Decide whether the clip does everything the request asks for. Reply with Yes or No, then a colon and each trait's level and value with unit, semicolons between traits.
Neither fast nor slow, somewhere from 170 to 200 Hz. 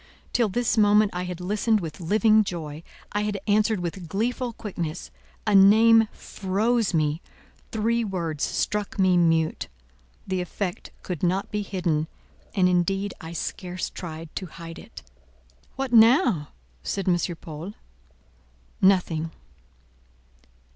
No: slow, 125 wpm; high, 190 Hz